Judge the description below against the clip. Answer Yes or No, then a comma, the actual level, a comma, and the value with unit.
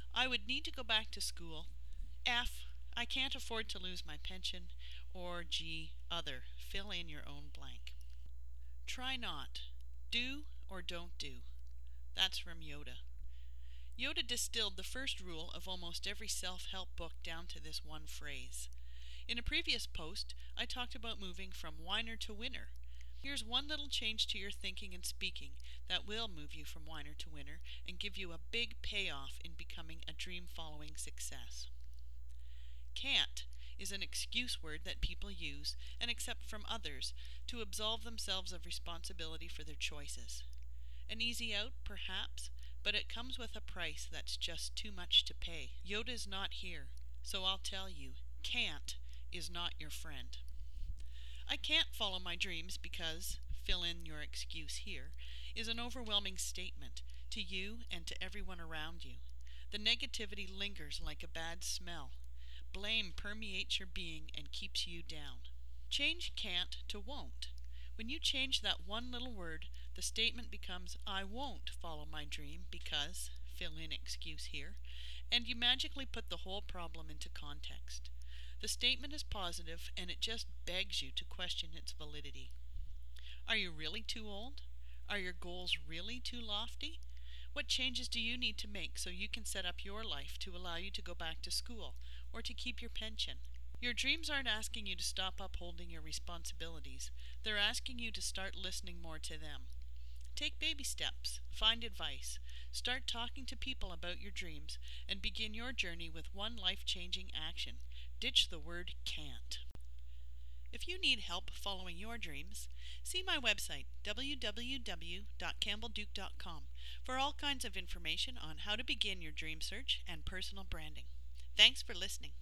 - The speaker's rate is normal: Yes, average, 160 wpm